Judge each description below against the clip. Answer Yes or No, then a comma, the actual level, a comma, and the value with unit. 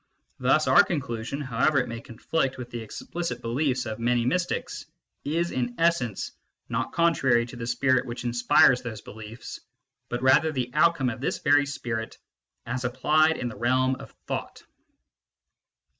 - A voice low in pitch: Yes, low, 125 Hz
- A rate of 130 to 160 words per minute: Yes, average, 155 wpm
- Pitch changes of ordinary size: Yes, average, 3.4 semitones